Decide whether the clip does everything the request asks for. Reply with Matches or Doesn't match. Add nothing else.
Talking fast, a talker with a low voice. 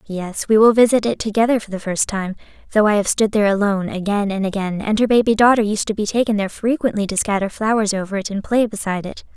Doesn't match